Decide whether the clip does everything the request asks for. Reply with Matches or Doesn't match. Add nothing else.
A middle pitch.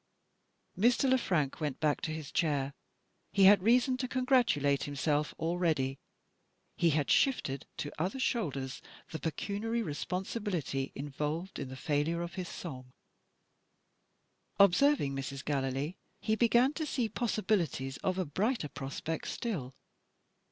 Matches